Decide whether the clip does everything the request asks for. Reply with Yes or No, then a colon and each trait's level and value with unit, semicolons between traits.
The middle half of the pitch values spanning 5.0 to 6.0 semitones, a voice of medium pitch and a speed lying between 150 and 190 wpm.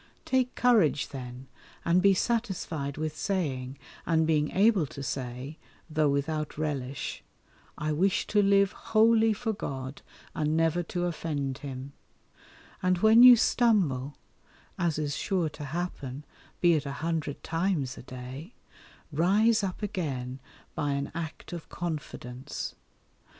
No: average, 5.3 semitones; medium, 155 Hz; slow, 135 wpm